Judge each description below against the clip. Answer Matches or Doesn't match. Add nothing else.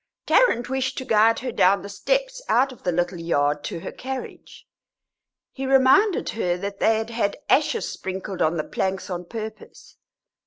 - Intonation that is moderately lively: Doesn't match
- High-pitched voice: Matches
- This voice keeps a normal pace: Matches